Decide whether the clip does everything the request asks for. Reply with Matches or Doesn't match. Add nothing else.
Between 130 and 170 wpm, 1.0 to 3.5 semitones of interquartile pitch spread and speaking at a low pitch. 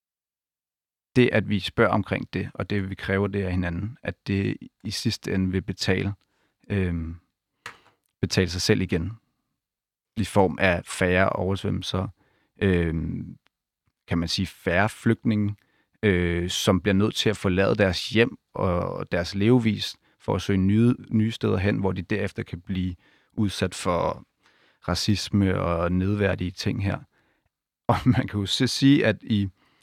Matches